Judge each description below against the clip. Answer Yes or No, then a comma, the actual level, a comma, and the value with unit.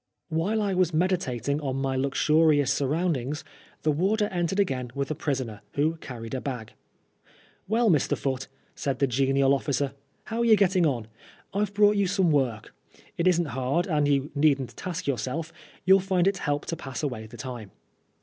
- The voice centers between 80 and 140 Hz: No, medium, 150 Hz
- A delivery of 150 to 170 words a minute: No, average, 185 wpm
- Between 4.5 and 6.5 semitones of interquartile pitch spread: Yes, average, 5.2 semitones